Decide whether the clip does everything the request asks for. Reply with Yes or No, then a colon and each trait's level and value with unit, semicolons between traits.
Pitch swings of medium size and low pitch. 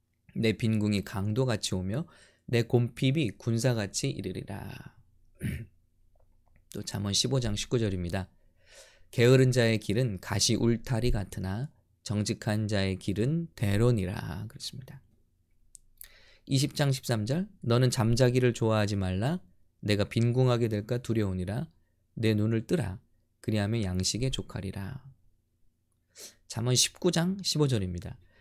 Yes: average, 4.5 semitones; low, 110 Hz